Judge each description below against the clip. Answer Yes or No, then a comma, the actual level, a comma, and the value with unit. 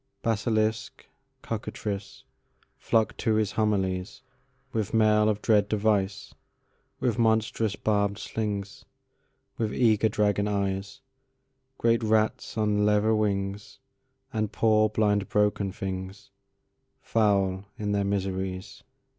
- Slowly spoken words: Yes, slow, 80 wpm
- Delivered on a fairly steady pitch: Yes, narrow, 1.8 semitones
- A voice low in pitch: Yes, low, 105 Hz